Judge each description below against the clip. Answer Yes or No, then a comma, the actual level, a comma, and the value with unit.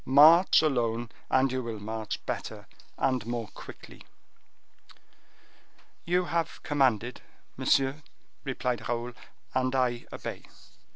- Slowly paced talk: Yes, slow, 105 wpm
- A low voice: Yes, low, 125 Hz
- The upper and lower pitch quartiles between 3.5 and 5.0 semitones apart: No, narrow, 2.6 semitones